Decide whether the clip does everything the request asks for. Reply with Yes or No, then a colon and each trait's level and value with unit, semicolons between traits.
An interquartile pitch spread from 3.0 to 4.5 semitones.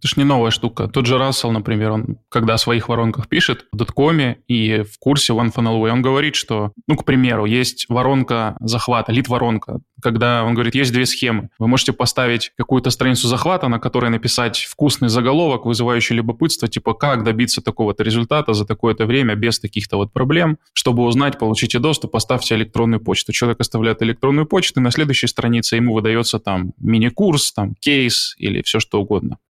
No: narrow, 2.4 semitones